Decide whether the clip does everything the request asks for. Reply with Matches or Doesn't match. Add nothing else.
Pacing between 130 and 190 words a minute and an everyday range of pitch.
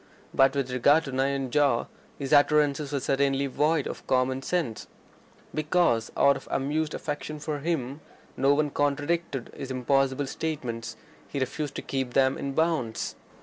Doesn't match